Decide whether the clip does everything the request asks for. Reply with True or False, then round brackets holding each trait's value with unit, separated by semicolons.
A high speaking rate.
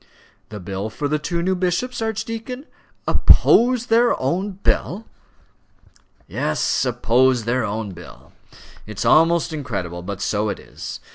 False (135 wpm)